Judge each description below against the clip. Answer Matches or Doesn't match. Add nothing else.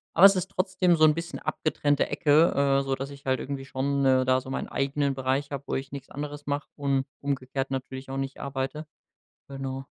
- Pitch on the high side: Doesn't match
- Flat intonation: Matches